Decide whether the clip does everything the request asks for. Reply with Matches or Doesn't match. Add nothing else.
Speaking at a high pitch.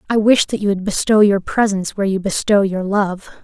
Matches